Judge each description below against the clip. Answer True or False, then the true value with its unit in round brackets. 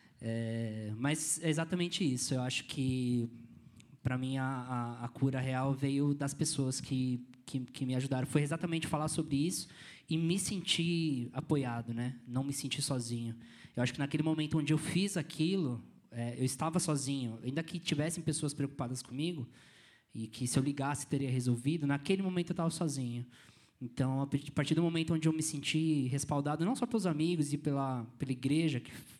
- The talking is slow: False (180 wpm)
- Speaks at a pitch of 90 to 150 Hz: True (140 Hz)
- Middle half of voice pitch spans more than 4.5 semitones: False (3.8 semitones)